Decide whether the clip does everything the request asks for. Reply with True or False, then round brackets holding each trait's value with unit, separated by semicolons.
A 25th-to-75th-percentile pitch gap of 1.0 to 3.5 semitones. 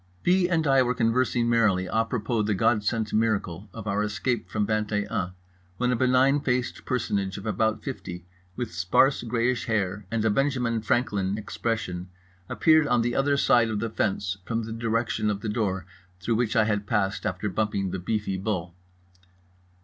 True (3.2 semitones)